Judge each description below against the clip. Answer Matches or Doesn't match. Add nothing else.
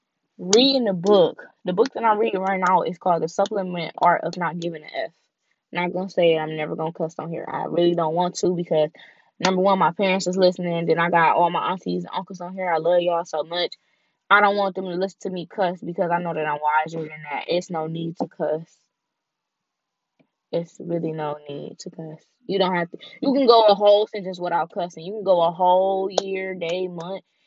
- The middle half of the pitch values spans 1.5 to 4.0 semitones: Matches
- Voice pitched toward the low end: Doesn't match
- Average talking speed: Doesn't match